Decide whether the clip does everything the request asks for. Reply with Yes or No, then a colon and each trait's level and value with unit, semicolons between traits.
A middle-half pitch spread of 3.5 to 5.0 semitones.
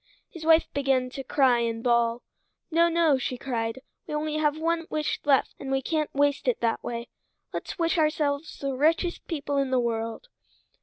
Yes: average, 3.9 semitones